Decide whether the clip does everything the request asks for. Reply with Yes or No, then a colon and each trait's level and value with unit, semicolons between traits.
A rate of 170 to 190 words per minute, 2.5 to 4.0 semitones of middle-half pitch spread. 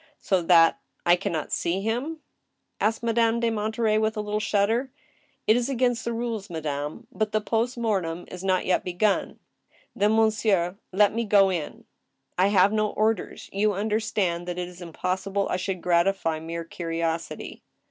Yes: average, 180 wpm; average, 3.7 semitones